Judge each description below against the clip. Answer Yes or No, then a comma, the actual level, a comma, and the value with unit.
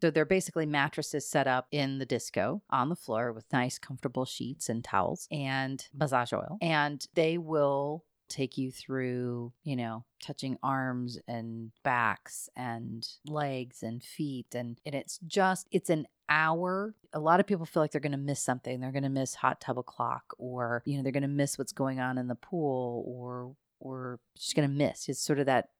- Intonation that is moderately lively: Yes, average, 3.5 semitones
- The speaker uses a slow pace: No, average, 200 wpm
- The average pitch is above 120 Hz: Yes, low, 135 Hz